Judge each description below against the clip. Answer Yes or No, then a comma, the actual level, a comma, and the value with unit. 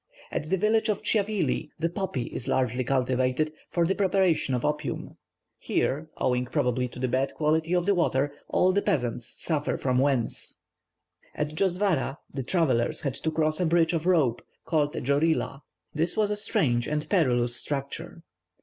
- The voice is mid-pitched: Yes, medium, 155 Hz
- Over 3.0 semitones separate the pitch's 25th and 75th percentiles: Yes, average, 5.1 semitones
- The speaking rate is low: No, average, 165 wpm